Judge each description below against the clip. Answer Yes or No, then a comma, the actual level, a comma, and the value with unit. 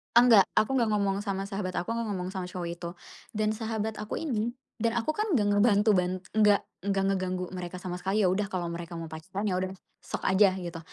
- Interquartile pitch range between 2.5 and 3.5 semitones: Yes, average, 2.9 semitones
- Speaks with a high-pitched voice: Yes, high, 195 Hz